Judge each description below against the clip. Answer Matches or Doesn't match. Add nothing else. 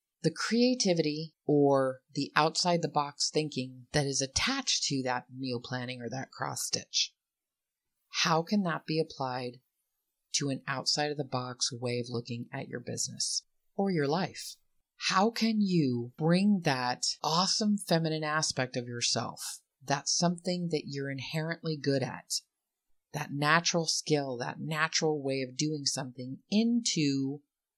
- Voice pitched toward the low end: Doesn't match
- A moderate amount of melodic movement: Matches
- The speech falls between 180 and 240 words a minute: Doesn't match